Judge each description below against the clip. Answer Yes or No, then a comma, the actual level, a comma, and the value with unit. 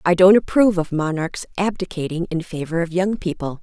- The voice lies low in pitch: No, medium, 175 Hz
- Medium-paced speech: Yes, average, 180 wpm